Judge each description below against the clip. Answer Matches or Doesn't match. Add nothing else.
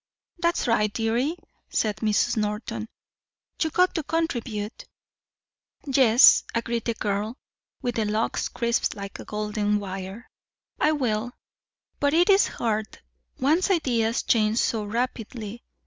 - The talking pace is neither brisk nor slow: Doesn't match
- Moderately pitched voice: Doesn't match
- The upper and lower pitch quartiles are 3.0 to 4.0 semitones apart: Matches